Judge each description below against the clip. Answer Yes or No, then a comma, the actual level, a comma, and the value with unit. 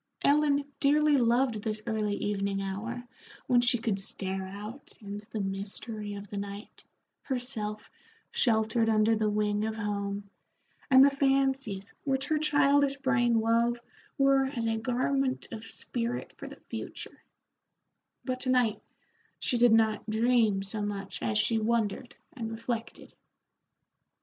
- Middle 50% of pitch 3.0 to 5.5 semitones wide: Yes, average, 3.6 semitones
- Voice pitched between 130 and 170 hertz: No, high, 225 Hz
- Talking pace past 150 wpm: No, average, 140 wpm